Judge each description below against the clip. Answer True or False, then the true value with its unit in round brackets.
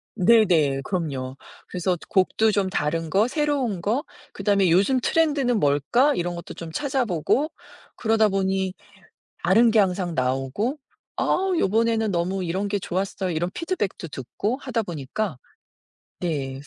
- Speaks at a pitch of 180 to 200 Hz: True (190 Hz)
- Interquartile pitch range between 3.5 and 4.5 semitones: False (5.2 semitones)